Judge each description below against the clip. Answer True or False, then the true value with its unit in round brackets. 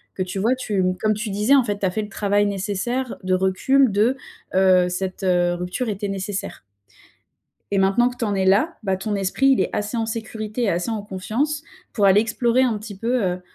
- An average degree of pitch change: True (3.4 semitones)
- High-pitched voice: True (205 Hz)